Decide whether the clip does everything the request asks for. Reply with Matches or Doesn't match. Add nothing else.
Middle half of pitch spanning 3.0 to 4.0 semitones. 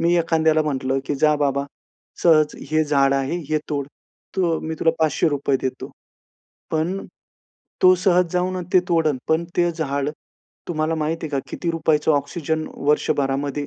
Doesn't match